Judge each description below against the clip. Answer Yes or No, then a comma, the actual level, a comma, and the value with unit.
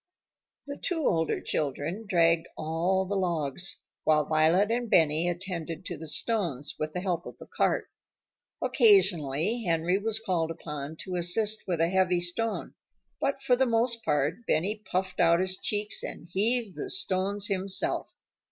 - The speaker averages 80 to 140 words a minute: No, average, 155 wpm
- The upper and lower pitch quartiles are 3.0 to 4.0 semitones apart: No, average, 4.4 semitones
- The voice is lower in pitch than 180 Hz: No, medium, 185 Hz